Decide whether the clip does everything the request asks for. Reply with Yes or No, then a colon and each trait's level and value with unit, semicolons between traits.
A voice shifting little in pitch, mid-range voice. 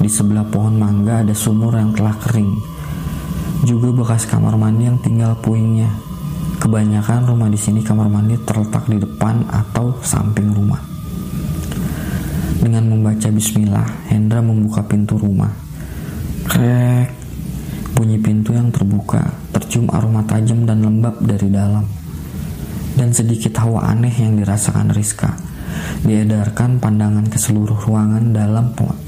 No: narrow, 1.7 semitones; low, 110 Hz